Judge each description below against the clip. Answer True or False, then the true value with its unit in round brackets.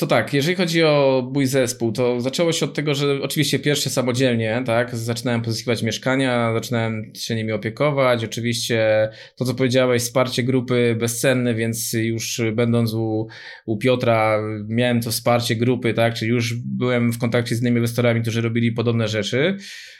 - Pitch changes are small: True (2.2 semitones)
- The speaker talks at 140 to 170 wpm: True (160 wpm)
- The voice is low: True (120 Hz)